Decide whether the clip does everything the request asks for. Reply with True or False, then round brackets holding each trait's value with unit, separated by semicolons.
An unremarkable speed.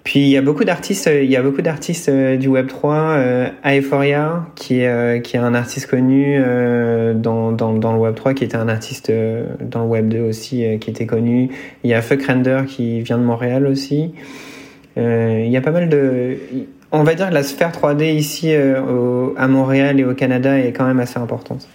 True (210 wpm)